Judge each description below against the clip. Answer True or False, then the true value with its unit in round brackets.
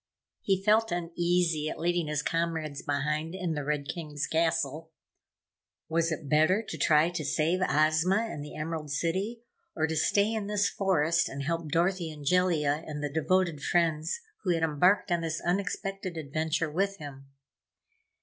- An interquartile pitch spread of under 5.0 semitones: True (3.1 semitones)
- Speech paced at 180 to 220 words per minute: False (160 wpm)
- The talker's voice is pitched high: False (165 Hz)